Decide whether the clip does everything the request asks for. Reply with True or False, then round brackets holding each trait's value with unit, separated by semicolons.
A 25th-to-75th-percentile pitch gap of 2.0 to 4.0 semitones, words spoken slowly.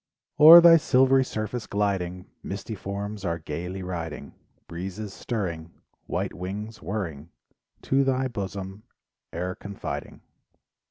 True (3.7 semitones; 110 wpm)